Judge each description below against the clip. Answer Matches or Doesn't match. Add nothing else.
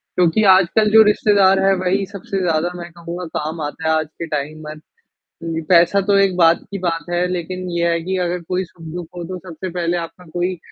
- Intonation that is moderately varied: Doesn't match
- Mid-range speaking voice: Matches